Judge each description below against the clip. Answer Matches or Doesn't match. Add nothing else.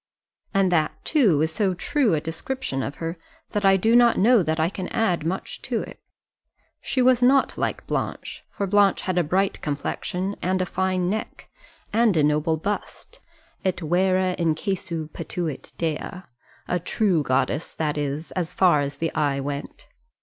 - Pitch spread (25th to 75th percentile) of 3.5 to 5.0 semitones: Matches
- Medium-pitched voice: Matches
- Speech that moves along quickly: Doesn't match